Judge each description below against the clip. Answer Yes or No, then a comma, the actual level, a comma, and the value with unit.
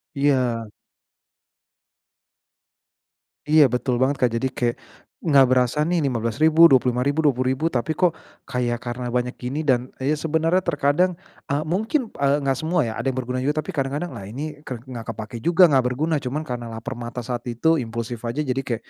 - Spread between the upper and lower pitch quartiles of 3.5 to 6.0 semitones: Yes, average, 4.1 semitones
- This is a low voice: Yes, low, 130 Hz